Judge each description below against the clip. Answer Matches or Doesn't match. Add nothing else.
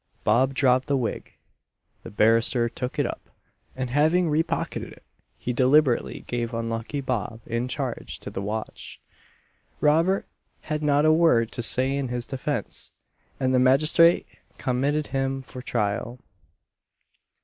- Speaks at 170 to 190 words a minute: Doesn't match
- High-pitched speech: Doesn't match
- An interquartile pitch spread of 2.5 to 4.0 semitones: Matches